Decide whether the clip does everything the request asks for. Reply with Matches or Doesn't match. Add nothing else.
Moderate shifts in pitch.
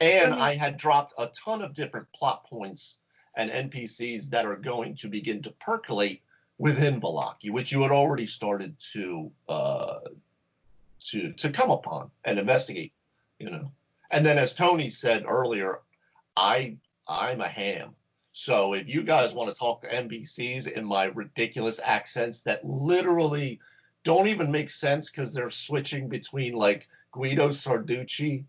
Matches